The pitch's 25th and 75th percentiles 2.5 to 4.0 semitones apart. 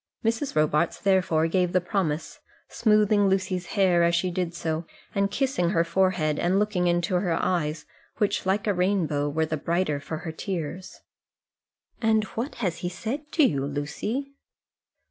Yes: average, 3.6 semitones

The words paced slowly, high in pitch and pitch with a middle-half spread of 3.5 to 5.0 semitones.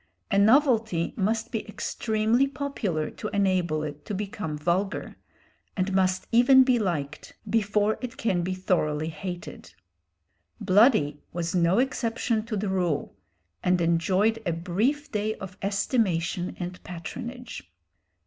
Yes: slow, 130 wpm; high, 195 Hz; average, 4.6 semitones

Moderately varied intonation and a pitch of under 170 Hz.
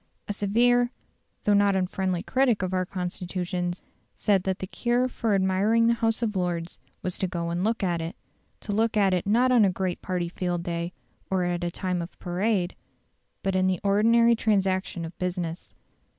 No: average, 3.2 semitones; high, 190 Hz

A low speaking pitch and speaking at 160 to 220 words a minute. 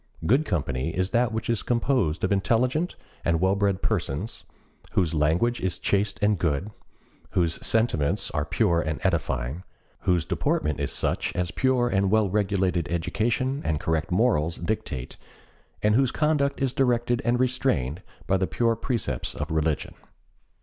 No: very low, 95 Hz; average, 150 wpm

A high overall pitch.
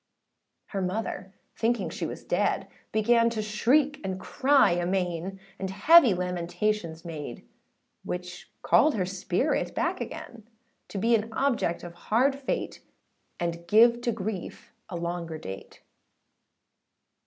Yes: high, 195 Hz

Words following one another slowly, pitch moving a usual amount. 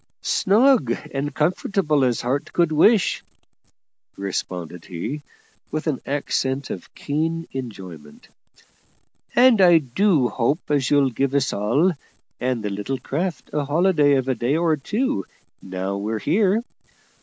No: slow, 130 wpm; wide, 5.7 semitones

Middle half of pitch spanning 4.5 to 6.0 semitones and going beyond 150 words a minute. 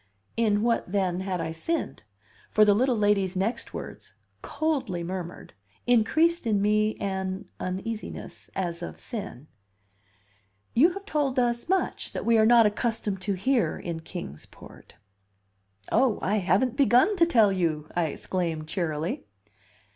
No: average, 4.9 semitones; average, 140 wpm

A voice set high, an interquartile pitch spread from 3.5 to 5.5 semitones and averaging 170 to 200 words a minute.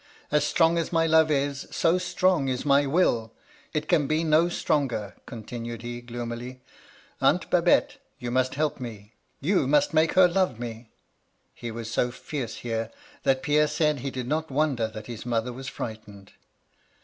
No: low, 130 Hz; average, 4.7 semitones; average, 175 wpm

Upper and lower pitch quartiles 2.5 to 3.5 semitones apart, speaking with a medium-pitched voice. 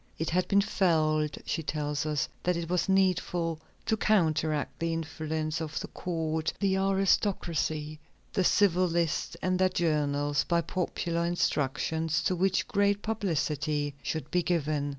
Yes: average, 3.1 semitones; medium, 165 Hz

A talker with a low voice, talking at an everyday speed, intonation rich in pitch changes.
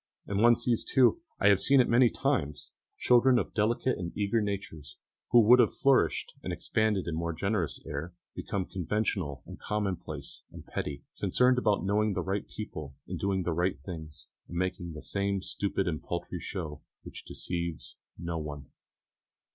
No: very low, 95 Hz; average, 170 wpm; average, 4.6 semitones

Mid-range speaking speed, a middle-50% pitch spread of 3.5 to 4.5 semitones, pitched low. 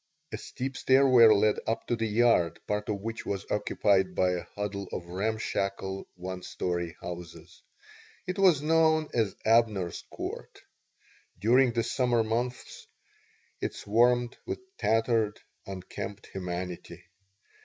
No: slow, 125 wpm; average, 4.0 semitones; low, 110 Hz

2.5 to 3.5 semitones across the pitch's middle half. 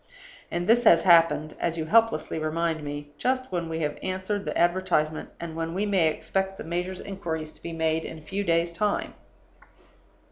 Yes: average, 3.0 semitones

